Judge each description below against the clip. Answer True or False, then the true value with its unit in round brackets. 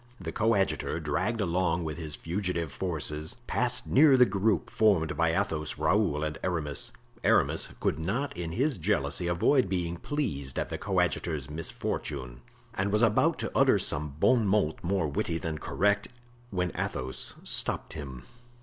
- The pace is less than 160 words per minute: True (150 wpm)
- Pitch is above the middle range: False (85 Hz)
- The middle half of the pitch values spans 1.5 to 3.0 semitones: False (4.8 semitones)